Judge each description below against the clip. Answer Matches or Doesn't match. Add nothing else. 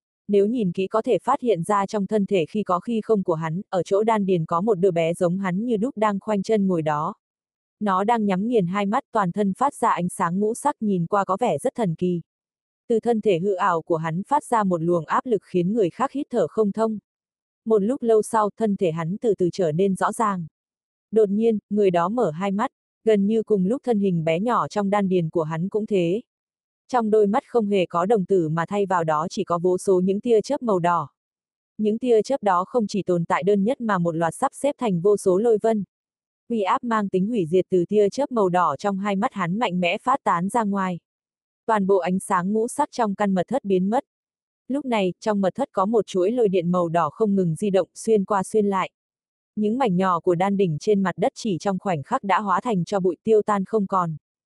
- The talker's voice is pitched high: Matches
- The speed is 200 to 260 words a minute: Matches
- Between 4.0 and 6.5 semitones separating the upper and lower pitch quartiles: Doesn't match